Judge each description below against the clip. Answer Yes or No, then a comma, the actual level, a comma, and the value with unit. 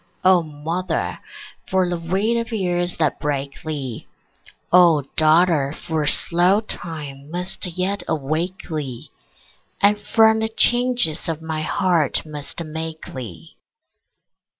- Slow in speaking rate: Yes, slow, 120 wpm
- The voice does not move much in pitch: No, average, 3.6 semitones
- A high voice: No, medium, 165 Hz